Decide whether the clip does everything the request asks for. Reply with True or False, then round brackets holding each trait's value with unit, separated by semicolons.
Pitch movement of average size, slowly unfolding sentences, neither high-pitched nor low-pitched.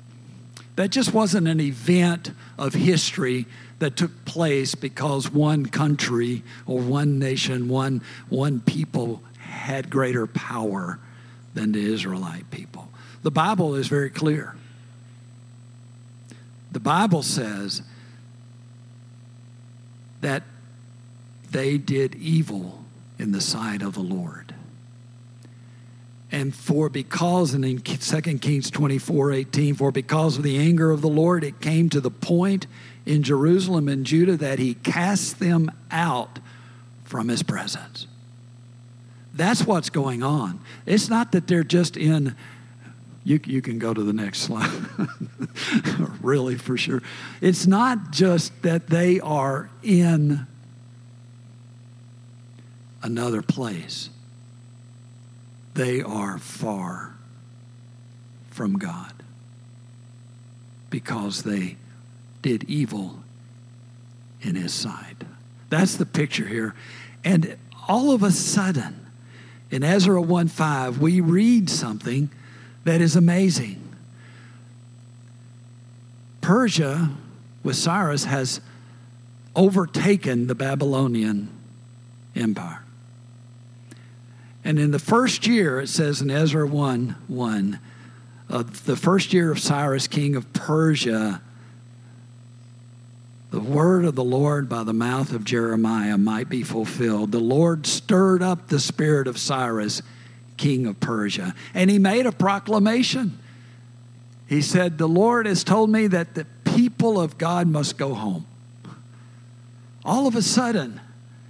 False (4.7 semitones; 115 wpm; 125 Hz)